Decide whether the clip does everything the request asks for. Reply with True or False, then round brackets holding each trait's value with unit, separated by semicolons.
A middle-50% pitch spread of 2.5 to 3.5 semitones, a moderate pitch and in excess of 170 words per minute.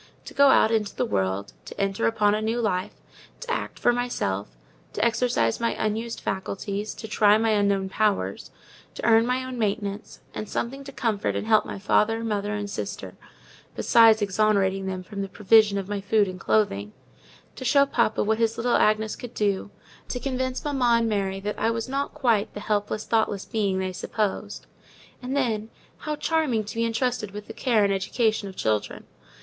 False (2.8 semitones; 215 Hz; 190 wpm)